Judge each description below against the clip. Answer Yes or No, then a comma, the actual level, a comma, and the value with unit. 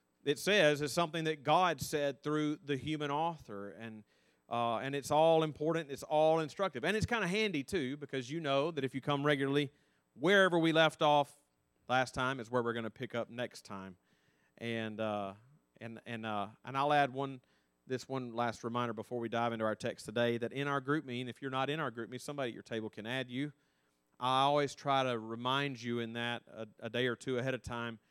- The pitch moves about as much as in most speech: Yes, average, 4.0 semitones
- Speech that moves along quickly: Yes, fast, 220 wpm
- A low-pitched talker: Yes, low, 130 Hz